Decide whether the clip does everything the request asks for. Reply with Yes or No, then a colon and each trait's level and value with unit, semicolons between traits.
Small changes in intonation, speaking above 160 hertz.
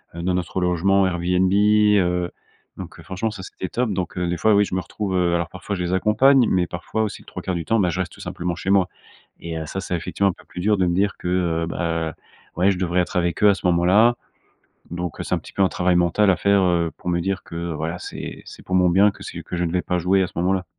No: narrow, 2.1 semitones; very low, 90 Hz